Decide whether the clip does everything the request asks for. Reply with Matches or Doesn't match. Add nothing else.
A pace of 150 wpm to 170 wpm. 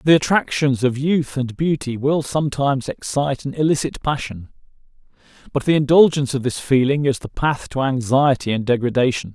Matches